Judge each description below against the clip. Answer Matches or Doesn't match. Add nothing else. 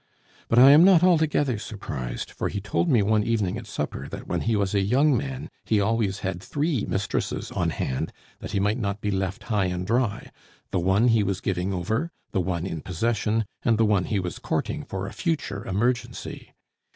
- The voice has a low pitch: Matches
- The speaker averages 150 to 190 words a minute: Doesn't match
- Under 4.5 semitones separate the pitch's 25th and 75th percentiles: Matches